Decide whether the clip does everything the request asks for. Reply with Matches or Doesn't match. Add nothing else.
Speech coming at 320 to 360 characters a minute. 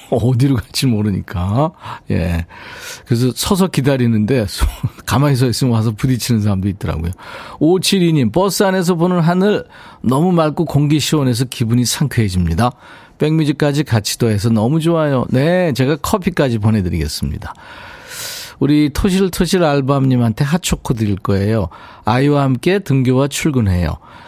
Matches